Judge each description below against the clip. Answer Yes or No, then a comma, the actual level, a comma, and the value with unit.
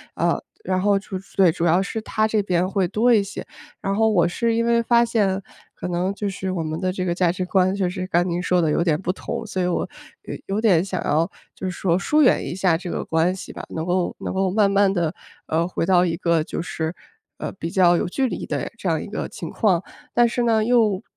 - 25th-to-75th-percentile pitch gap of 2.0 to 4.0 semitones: Yes, average, 3.2 semitones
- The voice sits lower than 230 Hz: Yes, medium, 185 Hz